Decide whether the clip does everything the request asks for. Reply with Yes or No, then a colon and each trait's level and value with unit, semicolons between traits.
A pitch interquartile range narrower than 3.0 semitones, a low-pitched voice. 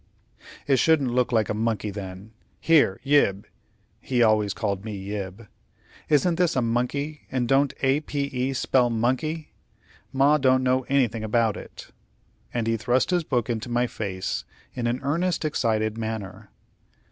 No: average, 4.1 semitones; low, 120 Hz